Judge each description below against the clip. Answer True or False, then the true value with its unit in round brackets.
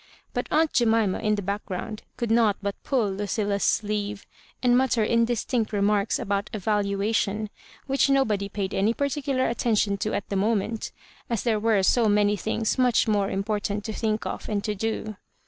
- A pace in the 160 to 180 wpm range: True (170 wpm)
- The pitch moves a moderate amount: False (2.3 semitones)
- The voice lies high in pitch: True (215 Hz)